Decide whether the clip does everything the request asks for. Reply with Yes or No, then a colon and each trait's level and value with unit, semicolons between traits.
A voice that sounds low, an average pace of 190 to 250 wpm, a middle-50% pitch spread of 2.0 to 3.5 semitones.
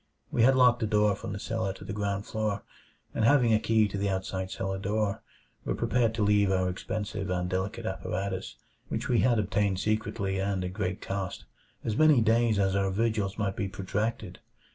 Yes: low, 105 Hz; average, 195 wpm; narrow, 2.5 semitones